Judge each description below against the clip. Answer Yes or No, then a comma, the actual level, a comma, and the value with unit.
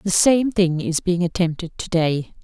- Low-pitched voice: No, medium, 180 Hz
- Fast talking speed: No, average, 195 wpm